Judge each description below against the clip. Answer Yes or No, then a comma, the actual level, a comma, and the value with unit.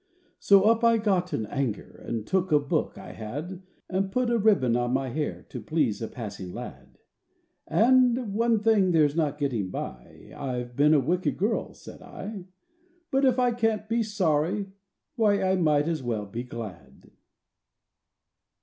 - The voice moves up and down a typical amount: No, wide, 8.7 semitones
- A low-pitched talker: No, medium, 175 Hz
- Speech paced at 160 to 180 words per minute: Yes, average, 165 wpm